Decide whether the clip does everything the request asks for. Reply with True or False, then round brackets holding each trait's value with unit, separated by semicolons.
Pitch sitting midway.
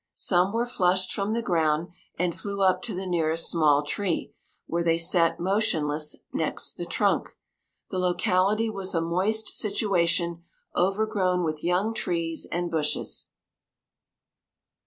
True (180 Hz)